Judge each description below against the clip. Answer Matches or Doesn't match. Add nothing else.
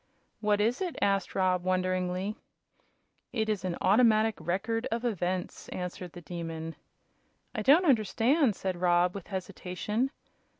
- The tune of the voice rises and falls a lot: Doesn't match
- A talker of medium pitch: Doesn't match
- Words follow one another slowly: Matches